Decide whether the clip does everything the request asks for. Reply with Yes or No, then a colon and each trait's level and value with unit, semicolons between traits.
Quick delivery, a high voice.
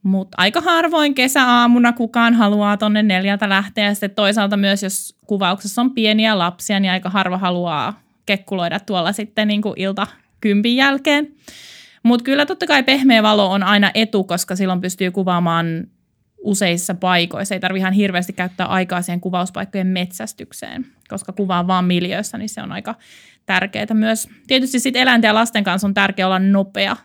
Yes: fast, 160 wpm; high, 205 Hz